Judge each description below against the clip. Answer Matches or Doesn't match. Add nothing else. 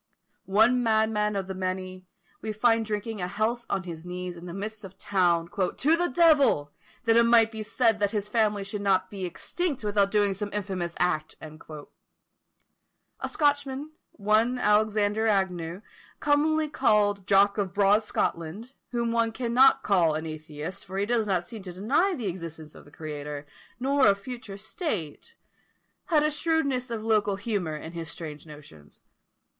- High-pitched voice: Matches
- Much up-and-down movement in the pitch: Doesn't match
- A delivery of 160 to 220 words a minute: Matches